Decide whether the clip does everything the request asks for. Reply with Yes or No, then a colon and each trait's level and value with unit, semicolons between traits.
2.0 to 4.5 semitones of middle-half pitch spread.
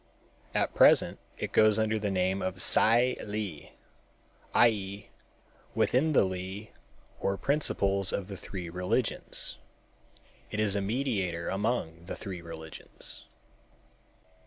Yes: average, 2.9 semitones